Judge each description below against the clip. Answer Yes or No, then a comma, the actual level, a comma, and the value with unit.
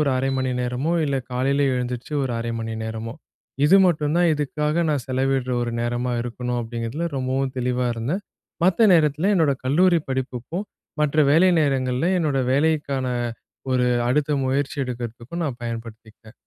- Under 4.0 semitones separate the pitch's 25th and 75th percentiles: Yes, average, 3.5 semitones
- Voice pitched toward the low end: Yes, low, 130 Hz